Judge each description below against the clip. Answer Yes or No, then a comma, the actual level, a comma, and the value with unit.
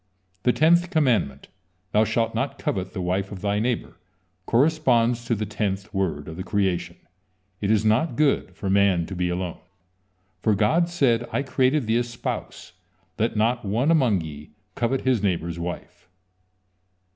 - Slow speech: No, average, 165 wpm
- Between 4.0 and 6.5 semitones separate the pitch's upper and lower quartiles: Yes, average, 4.6 semitones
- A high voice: No, low, 110 Hz